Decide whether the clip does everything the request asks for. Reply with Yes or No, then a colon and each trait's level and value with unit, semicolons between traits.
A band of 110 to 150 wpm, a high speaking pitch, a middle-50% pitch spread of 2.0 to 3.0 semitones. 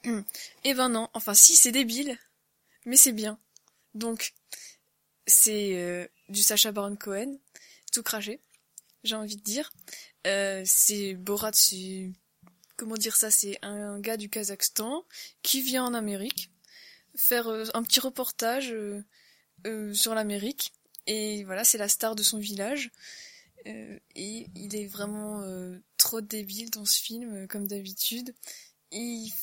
Yes: slow, 145 wpm; high, 215 Hz; narrow, 2.5 semitones